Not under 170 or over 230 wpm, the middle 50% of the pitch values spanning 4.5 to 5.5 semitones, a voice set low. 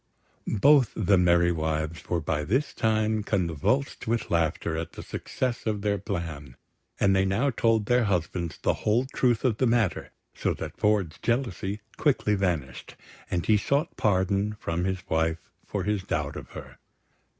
No: average, 160 wpm; average, 4.8 semitones; low, 100 Hz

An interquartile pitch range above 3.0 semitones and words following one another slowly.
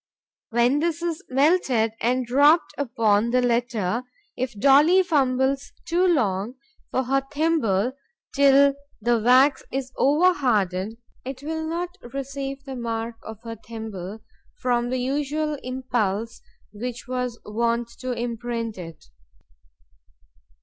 Yes: average, 3.5 semitones; slow, 120 wpm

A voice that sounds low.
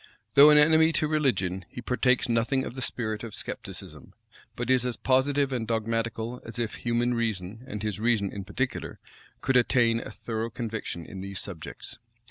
Yes: low, 115 Hz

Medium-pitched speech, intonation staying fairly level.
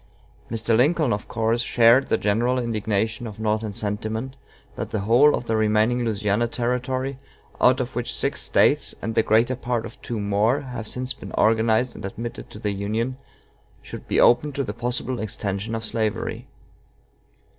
No: low, 115 Hz; narrow, 2.3 semitones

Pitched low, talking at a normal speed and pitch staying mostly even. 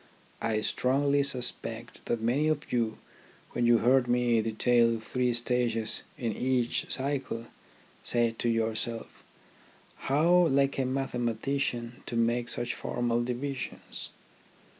No: low, 120 Hz; slow, 120 wpm; narrow, 2.3 semitones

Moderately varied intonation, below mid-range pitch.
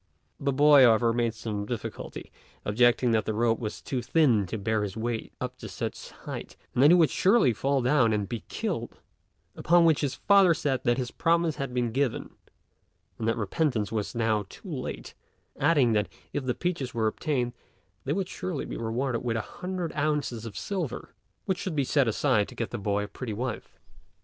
Yes: average, 4.8 semitones; low, 125 Hz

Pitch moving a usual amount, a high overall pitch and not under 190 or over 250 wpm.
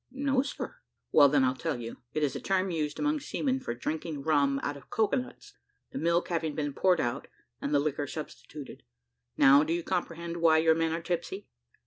No: average, 3.4 semitones; medium, 160 Hz; average, 200 wpm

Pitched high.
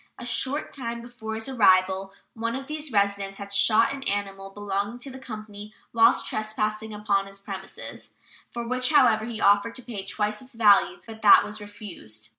Yes: high, 215 Hz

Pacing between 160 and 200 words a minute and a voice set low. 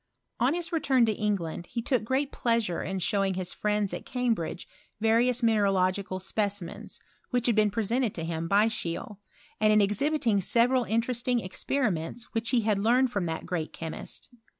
No: average, 170 wpm; high, 215 Hz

